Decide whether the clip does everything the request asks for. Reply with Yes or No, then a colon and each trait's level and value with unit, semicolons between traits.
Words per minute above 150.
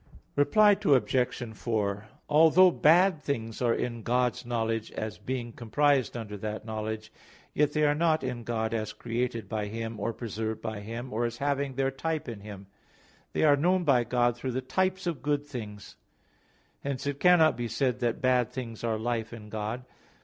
Yes: average, 180 wpm